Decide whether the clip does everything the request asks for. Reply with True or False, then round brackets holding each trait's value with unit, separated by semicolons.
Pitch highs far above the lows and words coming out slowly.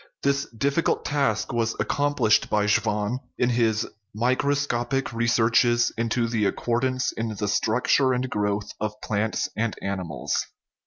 False (3.1 semitones; 130 wpm)